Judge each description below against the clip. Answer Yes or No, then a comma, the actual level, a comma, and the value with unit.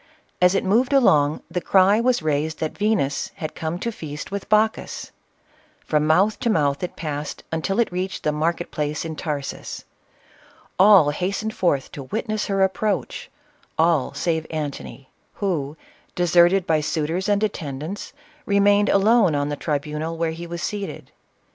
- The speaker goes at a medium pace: Yes, average, 160 wpm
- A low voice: No, medium, 170 Hz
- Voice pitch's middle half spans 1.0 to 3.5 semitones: No, average, 4.8 semitones